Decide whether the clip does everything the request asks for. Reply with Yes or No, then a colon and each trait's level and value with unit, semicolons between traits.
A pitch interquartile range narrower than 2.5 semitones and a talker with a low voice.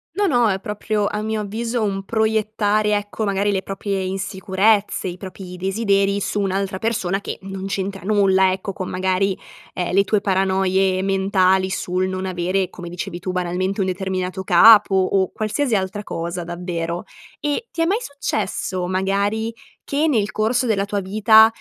No: narrow, 2.1 semitones; high, 195 Hz